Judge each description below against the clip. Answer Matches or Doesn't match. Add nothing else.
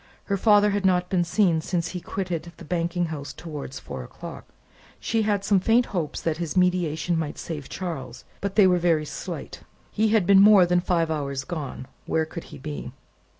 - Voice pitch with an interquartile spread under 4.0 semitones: Matches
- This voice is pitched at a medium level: Matches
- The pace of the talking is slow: Doesn't match